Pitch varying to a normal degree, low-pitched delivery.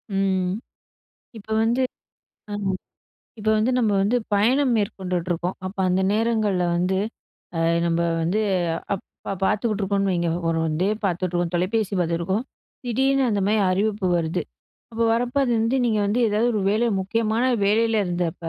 No: average, 3.7 semitones; high, 205 Hz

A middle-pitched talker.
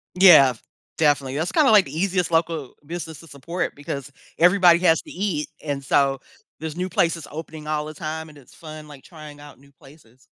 Yes: medium, 155 Hz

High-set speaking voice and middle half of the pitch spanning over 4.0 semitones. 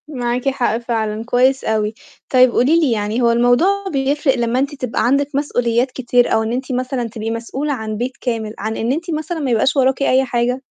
No: very high, 250 Hz; average, 2.7 semitones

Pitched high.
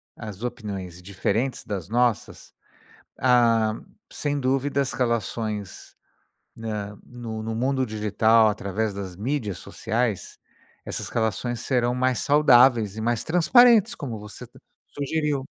No: low, 115 Hz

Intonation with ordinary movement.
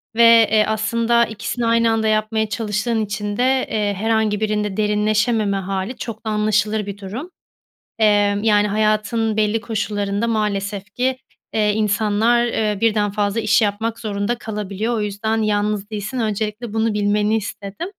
No: narrow, 1.4 semitones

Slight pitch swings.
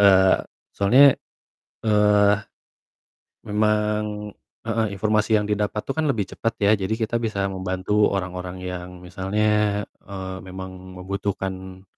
Yes: narrow, 2.2 semitones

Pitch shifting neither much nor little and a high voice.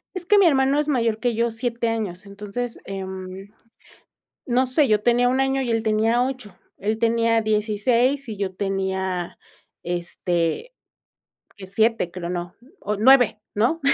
Yes: average, 4.0 semitones; high, 225 Hz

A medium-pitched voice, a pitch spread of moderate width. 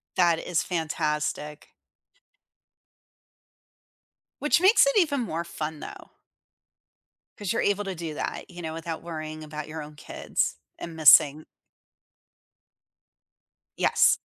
Yes: medium, 160 Hz; average, 3.1 semitones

